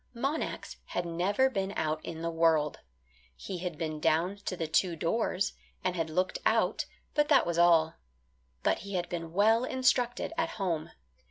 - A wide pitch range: No, average, 3.9 semitones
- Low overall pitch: No, medium, 175 Hz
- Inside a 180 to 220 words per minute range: No, average, 170 wpm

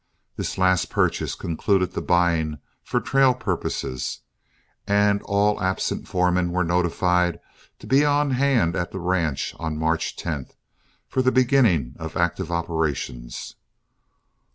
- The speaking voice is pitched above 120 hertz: No, very low, 90 Hz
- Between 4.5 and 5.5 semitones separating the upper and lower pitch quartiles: No, average, 3.8 semitones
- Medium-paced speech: No, slow, 130 wpm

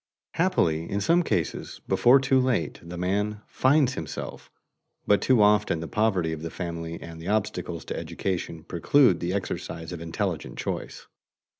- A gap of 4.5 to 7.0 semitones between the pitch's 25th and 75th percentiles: Yes, wide, 5.5 semitones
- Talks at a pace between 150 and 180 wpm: Yes, average, 155 wpm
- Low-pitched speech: Yes, very low, 95 Hz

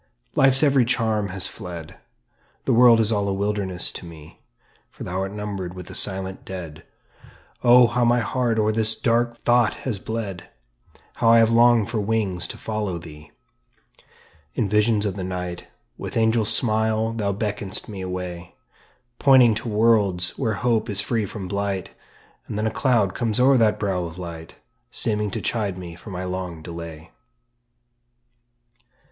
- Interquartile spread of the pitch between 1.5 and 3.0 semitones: No, average, 3.7 semitones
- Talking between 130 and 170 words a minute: Yes, average, 165 wpm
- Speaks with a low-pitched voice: Yes, low, 105 Hz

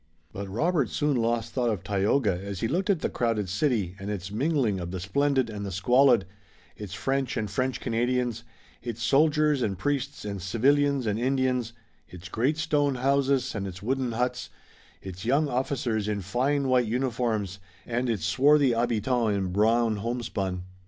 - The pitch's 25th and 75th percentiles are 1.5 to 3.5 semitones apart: No, average, 4.7 semitones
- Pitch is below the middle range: Yes, low, 120 Hz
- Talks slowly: No, average, 165 wpm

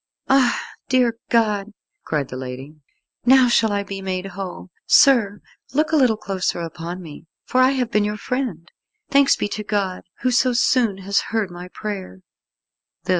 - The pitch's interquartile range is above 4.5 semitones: Yes, average, 5.2 semitones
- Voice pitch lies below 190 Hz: No, high, 205 Hz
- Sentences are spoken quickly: No, average, 165 wpm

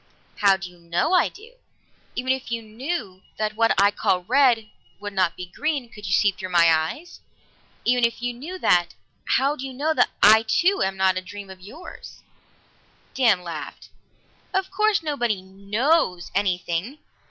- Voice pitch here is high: Yes, high, 215 Hz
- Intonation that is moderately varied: No, wide, 6.3 semitones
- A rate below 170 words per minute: No, average, 175 wpm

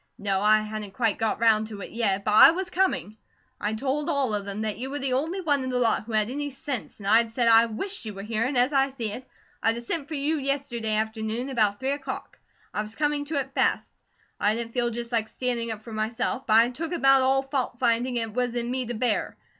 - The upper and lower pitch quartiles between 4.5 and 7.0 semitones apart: No, average, 3.8 semitones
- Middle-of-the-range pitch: No, high, 235 Hz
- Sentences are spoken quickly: Yes, fast, 250 wpm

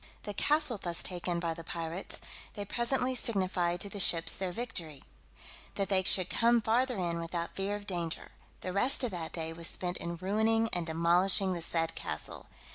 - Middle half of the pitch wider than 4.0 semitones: No, average, 3.7 semitones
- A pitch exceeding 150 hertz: Yes, medium, 185 Hz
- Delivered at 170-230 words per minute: Yes, average, 185 wpm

